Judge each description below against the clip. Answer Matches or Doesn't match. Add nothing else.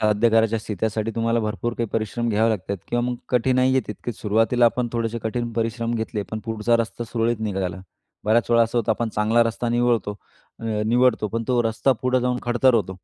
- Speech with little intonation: Matches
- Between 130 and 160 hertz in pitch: Doesn't match